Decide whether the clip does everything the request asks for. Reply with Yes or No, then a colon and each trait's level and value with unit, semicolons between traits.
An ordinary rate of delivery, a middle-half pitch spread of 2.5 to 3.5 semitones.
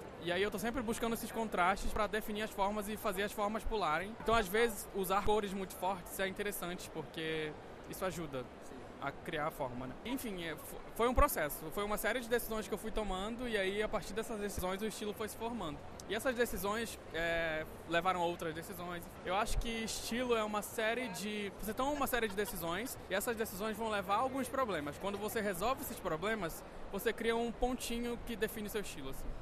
No: fast, 210 wpm; average, 3.1 semitones